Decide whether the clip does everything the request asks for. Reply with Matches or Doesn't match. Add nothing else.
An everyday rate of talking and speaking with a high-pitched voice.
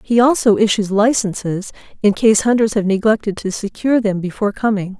Matches